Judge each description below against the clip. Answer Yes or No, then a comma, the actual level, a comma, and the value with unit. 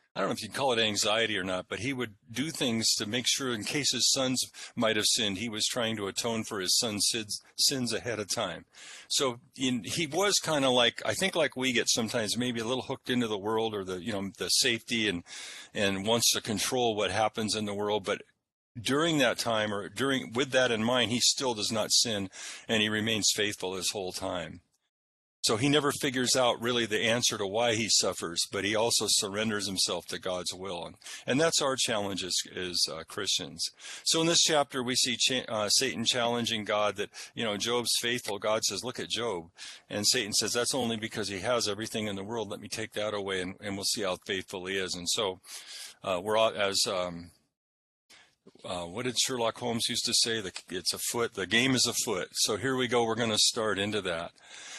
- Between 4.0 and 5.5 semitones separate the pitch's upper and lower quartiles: No, average, 3.4 semitones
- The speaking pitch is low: Yes, low, 115 Hz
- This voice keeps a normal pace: No, fast, 220 wpm